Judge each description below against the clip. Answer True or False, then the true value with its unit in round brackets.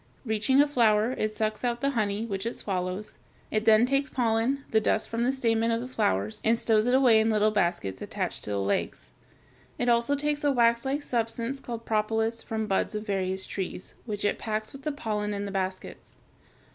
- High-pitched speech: True (225 Hz)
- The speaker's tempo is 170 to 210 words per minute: True (200 wpm)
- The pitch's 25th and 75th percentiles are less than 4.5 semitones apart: True (2.7 semitones)